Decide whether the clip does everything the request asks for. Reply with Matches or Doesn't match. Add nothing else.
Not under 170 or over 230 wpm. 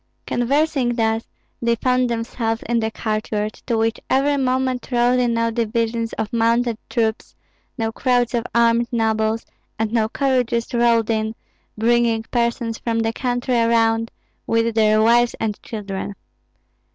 Doesn't match